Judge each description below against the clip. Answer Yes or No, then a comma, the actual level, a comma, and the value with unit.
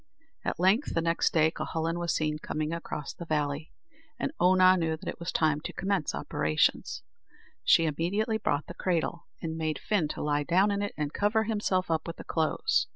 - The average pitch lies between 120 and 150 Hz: No, medium, 165 Hz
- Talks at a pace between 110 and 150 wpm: No, average, 195 wpm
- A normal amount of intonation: Yes, average, 3.3 semitones